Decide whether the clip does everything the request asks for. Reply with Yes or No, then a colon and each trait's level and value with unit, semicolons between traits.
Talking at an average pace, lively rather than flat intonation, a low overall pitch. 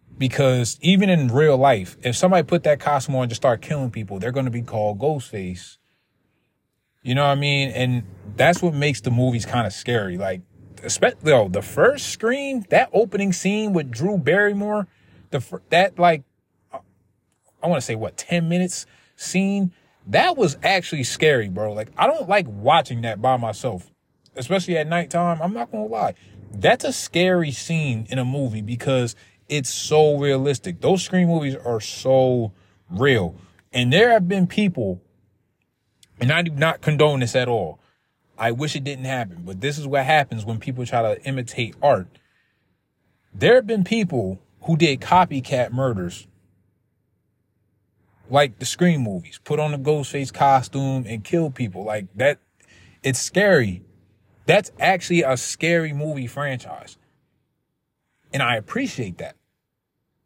Yes: average, 160 wpm; wide, 6.9 semitones; low, 130 Hz